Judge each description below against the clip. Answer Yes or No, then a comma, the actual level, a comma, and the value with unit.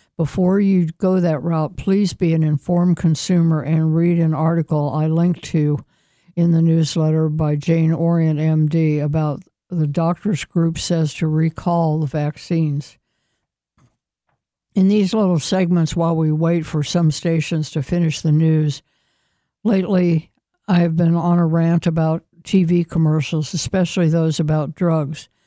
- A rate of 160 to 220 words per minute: No, average, 145 wpm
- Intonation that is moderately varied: No, narrow, 1.9 semitones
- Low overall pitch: No, medium, 165 Hz